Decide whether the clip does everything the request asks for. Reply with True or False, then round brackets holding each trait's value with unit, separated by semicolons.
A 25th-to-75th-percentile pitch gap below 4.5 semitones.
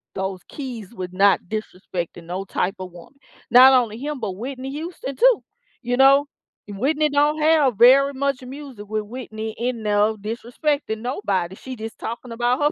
False (5.0 semitones)